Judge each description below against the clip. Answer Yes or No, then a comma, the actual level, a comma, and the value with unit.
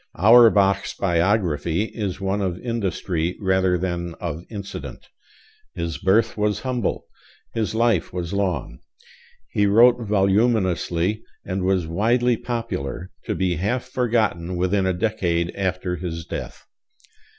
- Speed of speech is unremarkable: No, slow, 120 wpm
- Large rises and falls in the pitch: No, average, 3.8 semitones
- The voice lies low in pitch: Yes, very low, 95 Hz